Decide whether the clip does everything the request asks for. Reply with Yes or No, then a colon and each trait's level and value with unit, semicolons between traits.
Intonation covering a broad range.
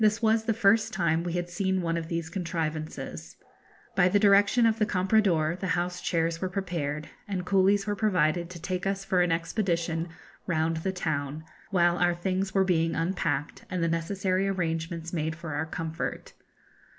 No: average, 2.9 semitones